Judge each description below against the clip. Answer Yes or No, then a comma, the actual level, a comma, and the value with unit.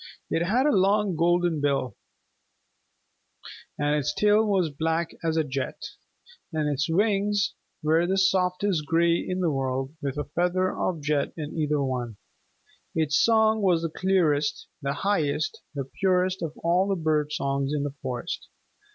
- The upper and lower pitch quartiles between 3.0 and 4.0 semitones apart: No, average, 4.4 semitones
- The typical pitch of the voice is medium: Yes, medium, 165 Hz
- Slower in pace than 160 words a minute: Yes, average, 150 wpm